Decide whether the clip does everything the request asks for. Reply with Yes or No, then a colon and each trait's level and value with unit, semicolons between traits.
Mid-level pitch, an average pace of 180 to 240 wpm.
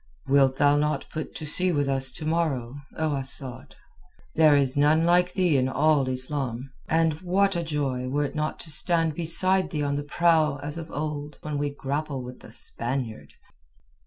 Yes: medium, 145 Hz; average, 185 wpm